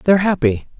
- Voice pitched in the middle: Yes, medium, 165 Hz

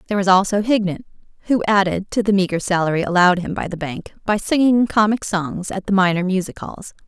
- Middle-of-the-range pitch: No, high, 195 Hz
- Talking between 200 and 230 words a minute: Yes, fast, 205 wpm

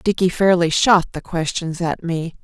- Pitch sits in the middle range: Yes, medium, 175 Hz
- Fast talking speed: No, average, 175 wpm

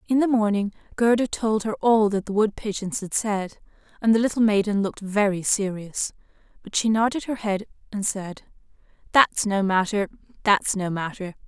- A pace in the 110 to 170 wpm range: Yes, average, 165 wpm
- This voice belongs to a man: No, female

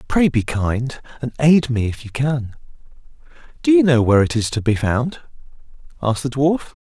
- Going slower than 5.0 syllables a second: No, 5.1 syllables/s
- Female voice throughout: No, male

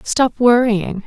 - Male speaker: No, female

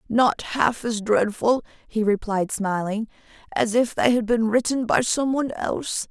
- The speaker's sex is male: No, female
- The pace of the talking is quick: No, average, 165 wpm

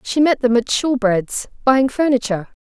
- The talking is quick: No, slow, 135 wpm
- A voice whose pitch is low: No, high, 245 Hz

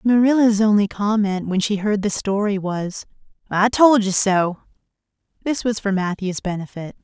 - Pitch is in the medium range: No, high, 205 Hz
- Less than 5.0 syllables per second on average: Yes, 4.7 syllables/s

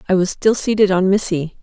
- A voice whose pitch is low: No, high, 190 Hz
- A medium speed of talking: No, fast, 220 wpm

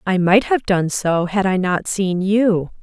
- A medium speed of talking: No, fast, 210 wpm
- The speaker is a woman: Yes, female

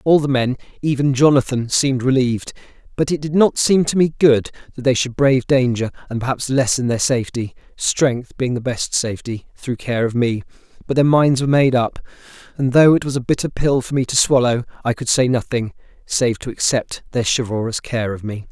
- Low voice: Yes, low, 130 Hz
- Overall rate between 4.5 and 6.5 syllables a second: Yes, 5.5 syllables/s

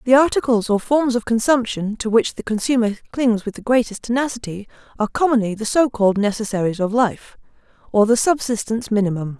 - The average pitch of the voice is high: Yes, high, 225 Hz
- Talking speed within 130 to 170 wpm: Yes, average, 165 wpm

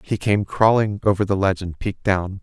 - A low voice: Yes, low, 100 Hz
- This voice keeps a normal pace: No, fast, 225 wpm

